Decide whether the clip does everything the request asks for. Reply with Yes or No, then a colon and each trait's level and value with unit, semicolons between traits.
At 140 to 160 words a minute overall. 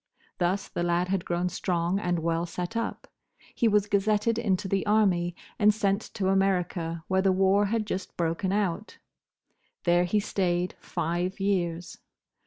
Yes: average, 155 wpm